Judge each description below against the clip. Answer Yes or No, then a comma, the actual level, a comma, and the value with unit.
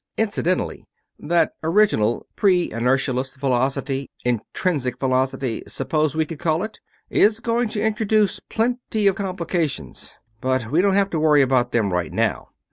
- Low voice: No, medium, 155 Hz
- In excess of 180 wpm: No, average, 140 wpm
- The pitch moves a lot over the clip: Yes, wide, 7.4 semitones